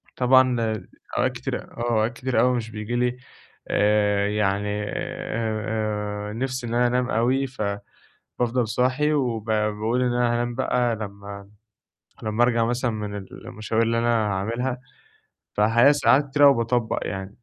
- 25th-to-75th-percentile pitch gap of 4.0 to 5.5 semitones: No, average, 2.8 semitones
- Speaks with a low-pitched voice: Yes, low, 115 Hz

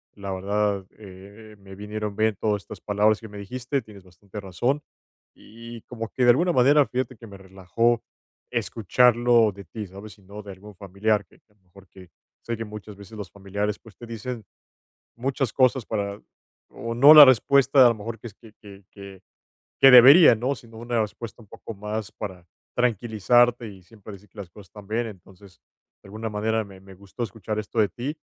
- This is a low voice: Yes, low, 105 Hz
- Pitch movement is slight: No, average, 3.1 semitones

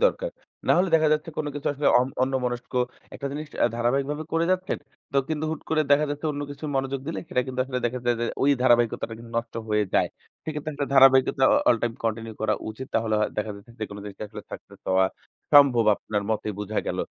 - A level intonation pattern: No, average, 4.2 semitones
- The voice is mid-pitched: No, low, 130 Hz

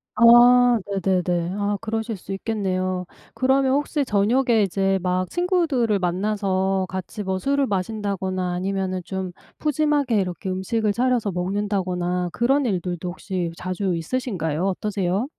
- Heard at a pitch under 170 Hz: No, high, 195 Hz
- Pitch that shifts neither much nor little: Yes, average, 4.2 semitones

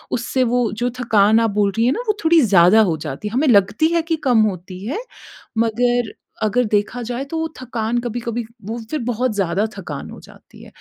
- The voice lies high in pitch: Yes, high, 230 Hz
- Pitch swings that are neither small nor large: Yes, average, 3.3 semitones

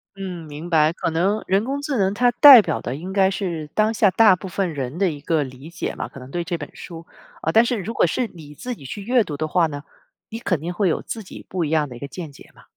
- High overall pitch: No, medium, 175 Hz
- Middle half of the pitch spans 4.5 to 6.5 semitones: Yes, average, 5.1 semitones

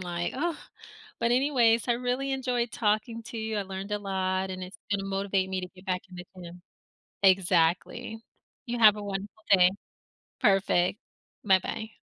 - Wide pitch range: No, average, 3.5 semitones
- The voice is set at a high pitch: Yes, high, 200 Hz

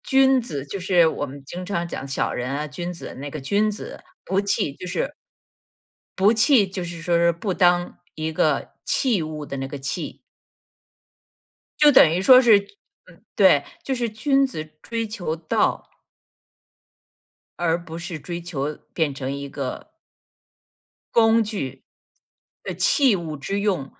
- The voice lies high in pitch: No, medium, 175 Hz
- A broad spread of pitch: Yes, wide, 5.8 semitones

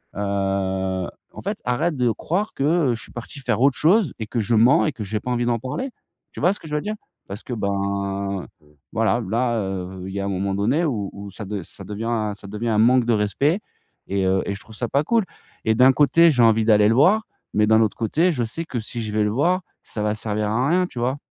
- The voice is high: No, low, 115 Hz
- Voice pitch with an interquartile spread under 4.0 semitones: No, average, 4.6 semitones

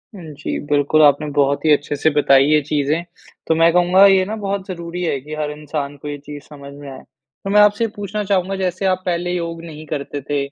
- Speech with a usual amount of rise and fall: Yes, average, 4.2 semitones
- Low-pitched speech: No, medium, 160 Hz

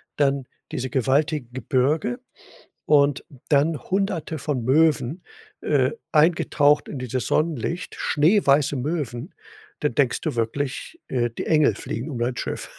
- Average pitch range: Yes, average, 3.5 semitones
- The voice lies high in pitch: No, medium, 145 Hz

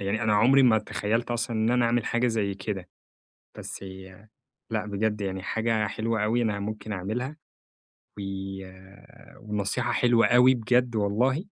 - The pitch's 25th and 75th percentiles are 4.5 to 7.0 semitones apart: No, average, 2.8 semitones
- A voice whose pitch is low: Yes, low, 110 Hz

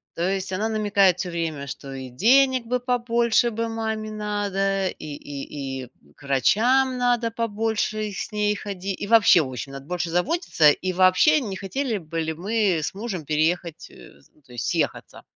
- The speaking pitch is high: Yes, high, 195 Hz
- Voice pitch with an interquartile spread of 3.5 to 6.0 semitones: Yes, wide, 5.6 semitones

